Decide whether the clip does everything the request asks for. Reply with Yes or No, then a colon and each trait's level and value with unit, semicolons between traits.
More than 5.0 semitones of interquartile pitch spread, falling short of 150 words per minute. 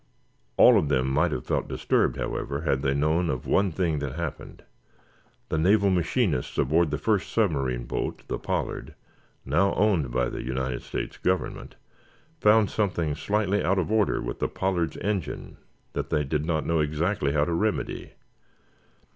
No: wide, 5.5 semitones; average, 165 wpm